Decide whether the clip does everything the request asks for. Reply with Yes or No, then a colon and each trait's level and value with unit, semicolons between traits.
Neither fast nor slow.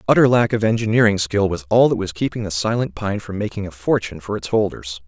No: fast, 235 wpm